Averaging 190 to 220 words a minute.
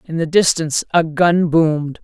No: average, 175 wpm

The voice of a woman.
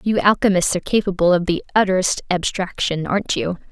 Yes: female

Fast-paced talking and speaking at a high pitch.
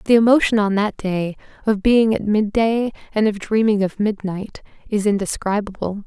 No: average, 170 wpm; high, 210 Hz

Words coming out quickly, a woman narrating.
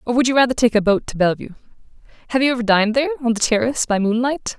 Yes: fast, 250 wpm; female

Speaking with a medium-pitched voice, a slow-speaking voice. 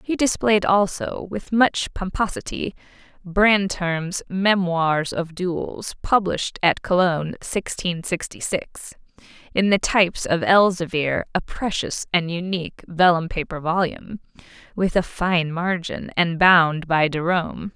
Yes: medium, 180 Hz; slow, 115 wpm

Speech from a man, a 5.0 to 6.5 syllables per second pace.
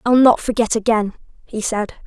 No: female; 5.2 syllables/s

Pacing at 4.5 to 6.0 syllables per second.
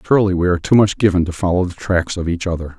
No: 7.2 syllables/s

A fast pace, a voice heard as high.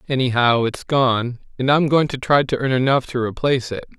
No: fast, 210 wpm; low, 130 Hz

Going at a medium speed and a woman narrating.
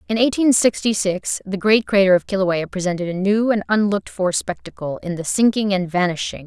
No: fast, 240 wpm; female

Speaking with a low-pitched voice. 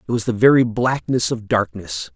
Yes: low, 115 Hz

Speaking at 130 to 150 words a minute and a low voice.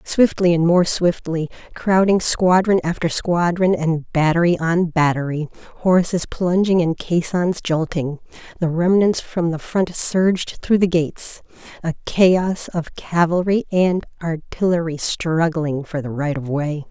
No: slow, 135 wpm; medium, 170 Hz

